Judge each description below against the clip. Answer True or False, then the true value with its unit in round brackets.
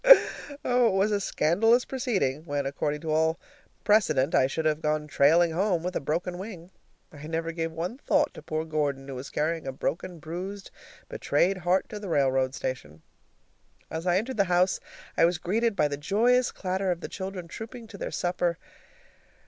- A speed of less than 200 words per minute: True (185 wpm)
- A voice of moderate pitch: True (170 Hz)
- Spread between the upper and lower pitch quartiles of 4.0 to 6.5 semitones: True (4.3 semitones)